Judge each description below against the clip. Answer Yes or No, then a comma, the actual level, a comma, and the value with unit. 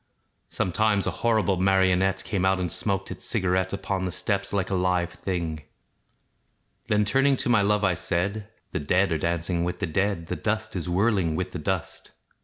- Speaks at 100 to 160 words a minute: No, average, 185 wpm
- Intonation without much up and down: Yes, narrow, 2.3 semitones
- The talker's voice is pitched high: No, very low, 95 Hz